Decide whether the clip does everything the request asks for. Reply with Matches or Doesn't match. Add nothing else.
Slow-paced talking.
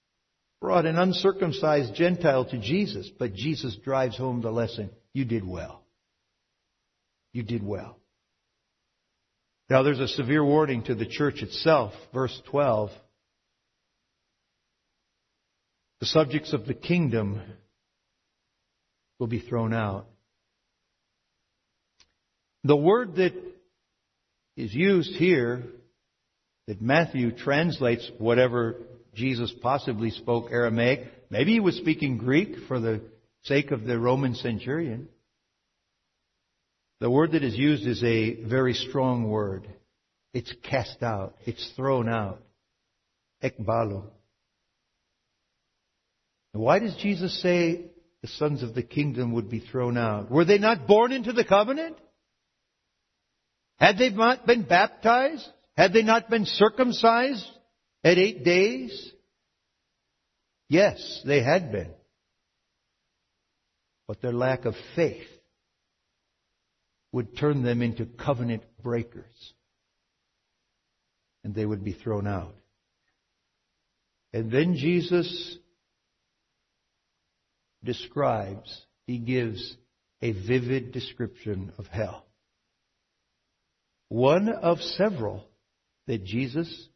Matches